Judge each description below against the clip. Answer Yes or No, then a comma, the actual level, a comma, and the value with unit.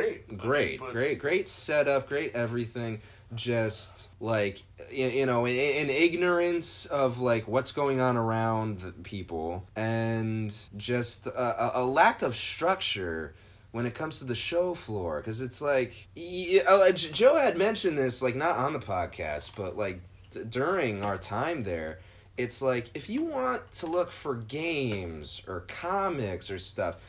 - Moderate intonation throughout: No, wide, 6.7 semitones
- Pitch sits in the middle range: No, low, 120 Hz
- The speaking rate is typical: Yes, average, 145 wpm